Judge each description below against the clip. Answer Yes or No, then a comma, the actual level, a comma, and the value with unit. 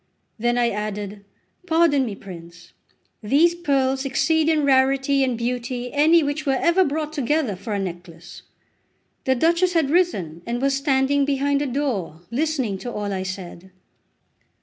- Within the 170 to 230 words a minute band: No, average, 150 wpm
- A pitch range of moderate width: No, wide, 6.0 semitones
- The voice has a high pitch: Yes, very high, 265 Hz